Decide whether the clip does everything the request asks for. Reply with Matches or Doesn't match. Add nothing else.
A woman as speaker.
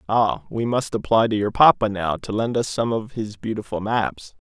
Doesn't match